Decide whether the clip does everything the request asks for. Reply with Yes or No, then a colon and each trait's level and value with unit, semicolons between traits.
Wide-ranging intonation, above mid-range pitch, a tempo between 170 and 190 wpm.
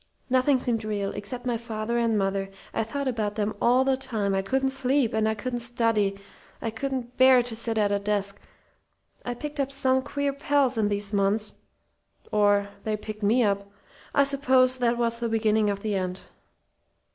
No: average, 3.8 semitones; high, 230 Hz; average, 185 wpm